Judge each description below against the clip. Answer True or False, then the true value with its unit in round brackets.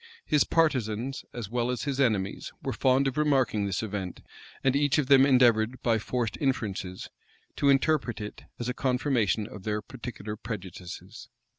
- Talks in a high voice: False (120 Hz)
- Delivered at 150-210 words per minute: True (160 wpm)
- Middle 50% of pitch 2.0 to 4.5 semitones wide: True (4.2 semitones)